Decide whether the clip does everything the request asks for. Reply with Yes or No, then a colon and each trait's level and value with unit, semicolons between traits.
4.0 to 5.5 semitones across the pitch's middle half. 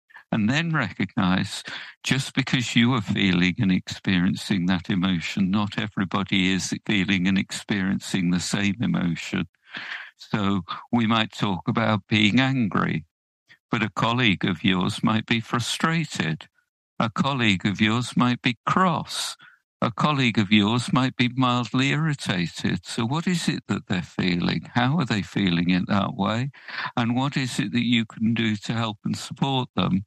Yes: average, 4.8 semitones